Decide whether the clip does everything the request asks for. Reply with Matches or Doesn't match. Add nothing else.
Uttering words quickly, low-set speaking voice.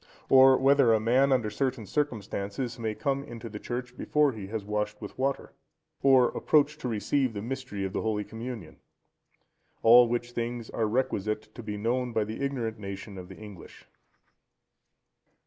Doesn't match